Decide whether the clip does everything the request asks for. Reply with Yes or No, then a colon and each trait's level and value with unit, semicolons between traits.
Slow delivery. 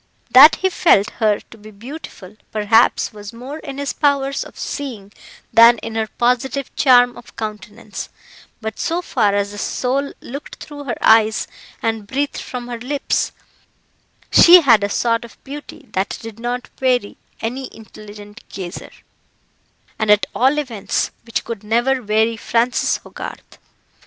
No: average, 150 wpm